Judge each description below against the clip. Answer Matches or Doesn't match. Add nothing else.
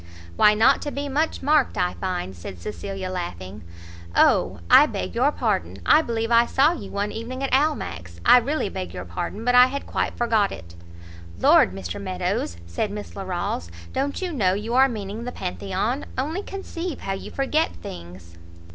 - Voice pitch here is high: Matches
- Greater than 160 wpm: Matches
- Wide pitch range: Matches